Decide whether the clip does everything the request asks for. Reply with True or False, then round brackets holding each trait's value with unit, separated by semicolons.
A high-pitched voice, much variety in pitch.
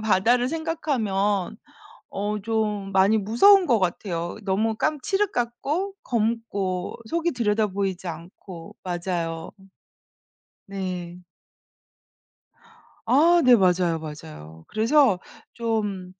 False (205 Hz; 4.7 semitones)